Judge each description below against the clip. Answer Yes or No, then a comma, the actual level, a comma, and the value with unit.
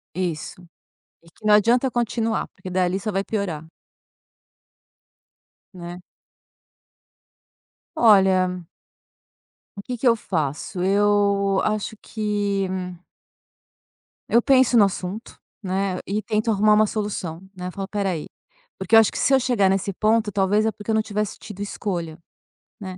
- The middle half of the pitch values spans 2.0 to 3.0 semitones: Yes, average, 2.7 semitones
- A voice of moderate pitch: No, high, 200 Hz